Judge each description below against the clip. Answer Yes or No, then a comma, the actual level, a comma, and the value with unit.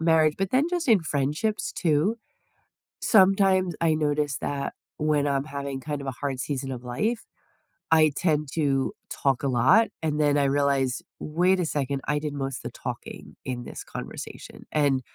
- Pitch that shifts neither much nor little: Yes, average, 3.4 semitones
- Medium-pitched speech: Yes, medium, 150 Hz